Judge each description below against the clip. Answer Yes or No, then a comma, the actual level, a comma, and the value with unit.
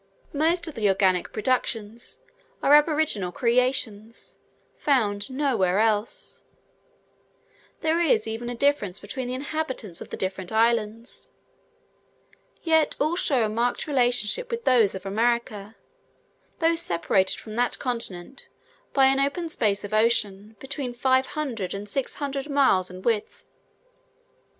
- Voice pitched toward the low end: No, high, 235 Hz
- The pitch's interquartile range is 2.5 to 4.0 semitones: No, average, 5.2 semitones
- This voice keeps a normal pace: No, slow, 125 wpm